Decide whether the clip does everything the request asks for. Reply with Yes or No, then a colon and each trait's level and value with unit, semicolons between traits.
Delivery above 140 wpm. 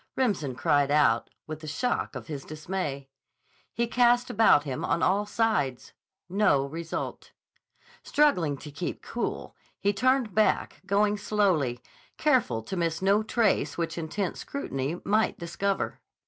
No: slow, 135 wpm